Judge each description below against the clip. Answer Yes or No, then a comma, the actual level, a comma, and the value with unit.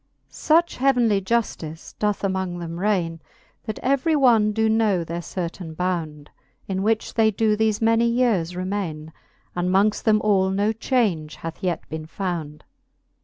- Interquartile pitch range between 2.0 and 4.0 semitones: No, average, 4.4 semitones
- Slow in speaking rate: No, average, 150 wpm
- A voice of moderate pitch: No, high, 195 Hz